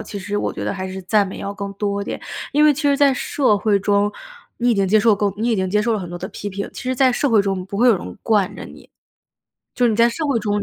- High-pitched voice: Yes, high, 205 Hz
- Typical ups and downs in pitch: Yes, average, 3.3 semitones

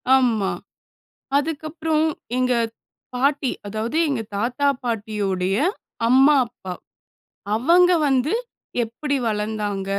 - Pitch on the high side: Yes, high, 245 Hz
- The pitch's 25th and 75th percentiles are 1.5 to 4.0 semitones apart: No, average, 5.2 semitones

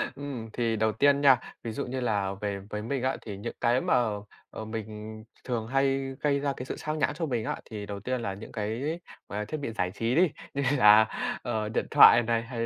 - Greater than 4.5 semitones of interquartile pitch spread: No, average, 3.8 semitones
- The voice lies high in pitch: No, low, 115 Hz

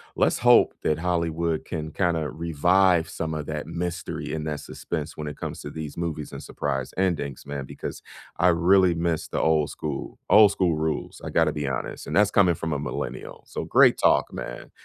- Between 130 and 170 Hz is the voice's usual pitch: No, very low, 80 Hz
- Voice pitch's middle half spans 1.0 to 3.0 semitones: Yes, narrow, 2.5 semitones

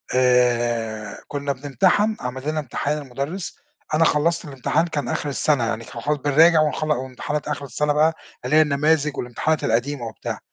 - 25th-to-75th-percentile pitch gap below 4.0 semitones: Yes, average, 3.4 semitones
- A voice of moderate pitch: Yes, medium, 145 Hz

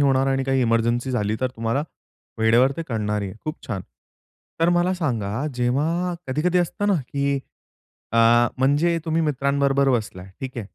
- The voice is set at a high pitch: No, low, 135 Hz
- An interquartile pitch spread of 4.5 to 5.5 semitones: Yes, average, 4.9 semitones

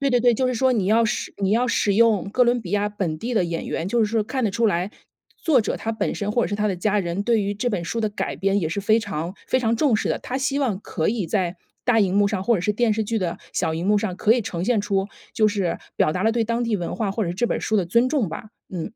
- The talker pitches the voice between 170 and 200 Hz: No, high, 210 Hz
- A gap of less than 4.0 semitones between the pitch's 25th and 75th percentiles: Yes, average, 3.3 semitones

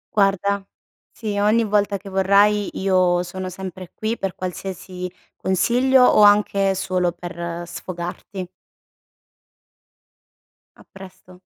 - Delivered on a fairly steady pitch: Yes, narrow, 2.0 semitones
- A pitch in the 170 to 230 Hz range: Yes, high, 190 Hz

